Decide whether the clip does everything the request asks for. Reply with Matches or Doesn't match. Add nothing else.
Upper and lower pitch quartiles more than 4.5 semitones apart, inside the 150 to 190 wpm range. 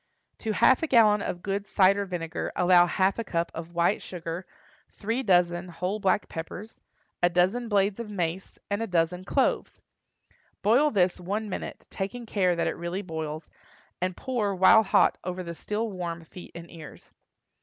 Doesn't match